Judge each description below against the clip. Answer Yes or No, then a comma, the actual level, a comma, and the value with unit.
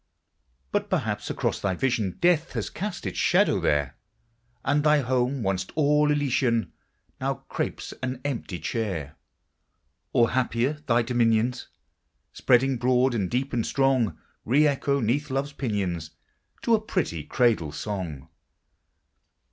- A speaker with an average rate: No, slow, 130 wpm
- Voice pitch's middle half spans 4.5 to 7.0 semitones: Yes, average, 5.2 semitones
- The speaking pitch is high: No, low, 125 Hz